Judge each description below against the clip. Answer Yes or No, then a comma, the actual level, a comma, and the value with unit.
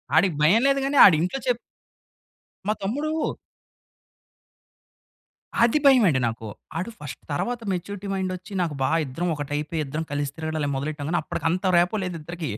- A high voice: No, medium, 175 Hz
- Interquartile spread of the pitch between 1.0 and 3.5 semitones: No, wide, 5.4 semitones